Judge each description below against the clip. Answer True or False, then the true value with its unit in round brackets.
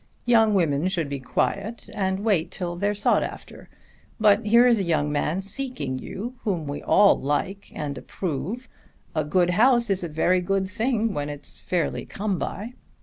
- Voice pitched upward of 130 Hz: True (190 Hz)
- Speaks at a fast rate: False (175 wpm)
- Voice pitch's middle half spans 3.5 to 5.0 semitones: False (5.4 semitones)